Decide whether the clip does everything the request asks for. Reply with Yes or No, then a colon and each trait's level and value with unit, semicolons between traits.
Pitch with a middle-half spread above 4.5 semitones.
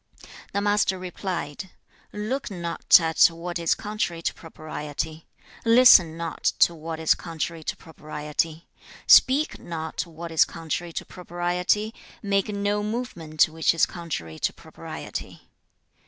No: average, 3.9 semitones